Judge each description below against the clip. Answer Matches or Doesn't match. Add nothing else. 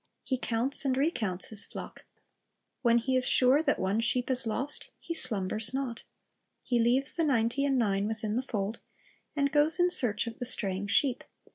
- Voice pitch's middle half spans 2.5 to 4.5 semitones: Matches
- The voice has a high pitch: Matches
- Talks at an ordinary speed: Matches